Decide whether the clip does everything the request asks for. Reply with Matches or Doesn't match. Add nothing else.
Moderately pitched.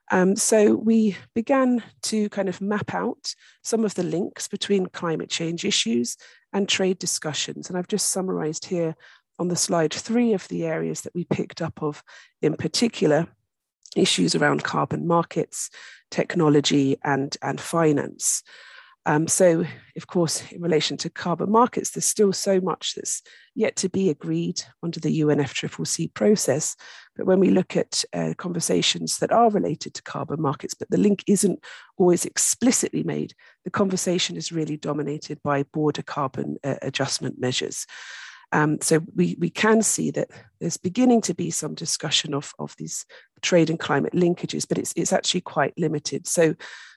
Matches